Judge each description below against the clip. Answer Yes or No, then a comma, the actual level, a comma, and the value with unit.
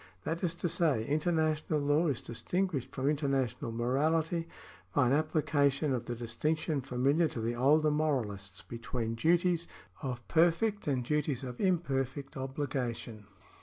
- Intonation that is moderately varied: Yes, average, 4.3 semitones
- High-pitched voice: No, medium, 140 Hz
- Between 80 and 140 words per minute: Yes, slow, 135 wpm